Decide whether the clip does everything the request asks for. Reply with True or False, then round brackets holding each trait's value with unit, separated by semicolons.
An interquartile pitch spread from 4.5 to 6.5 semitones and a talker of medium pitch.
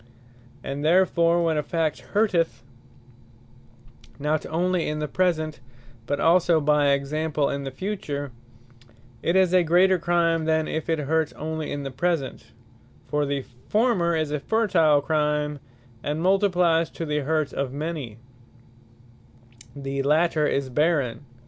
False (2.8 semitones; 155 Hz)